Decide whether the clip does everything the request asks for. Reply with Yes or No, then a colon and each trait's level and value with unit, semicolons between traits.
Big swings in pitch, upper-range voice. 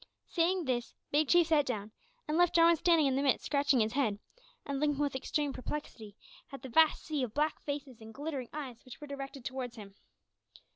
No: average, 3.1 semitones; very high, 280 Hz